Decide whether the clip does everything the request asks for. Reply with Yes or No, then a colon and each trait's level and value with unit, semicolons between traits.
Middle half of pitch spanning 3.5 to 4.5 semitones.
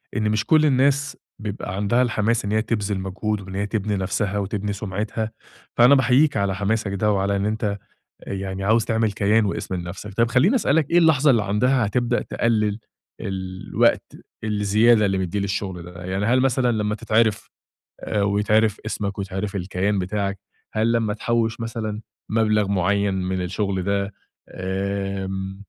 No: narrow, 2.6 semitones